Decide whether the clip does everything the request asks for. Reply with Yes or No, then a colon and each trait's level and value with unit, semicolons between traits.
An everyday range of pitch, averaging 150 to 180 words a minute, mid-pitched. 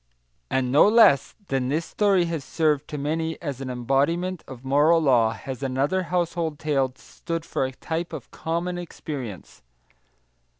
Yes: average, 4.1 semitones; average, 160 wpm; medium, 150 Hz